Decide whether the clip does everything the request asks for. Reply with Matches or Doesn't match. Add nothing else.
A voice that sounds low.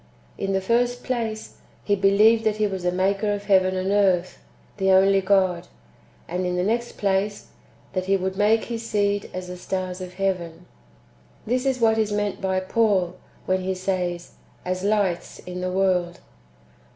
Doesn't match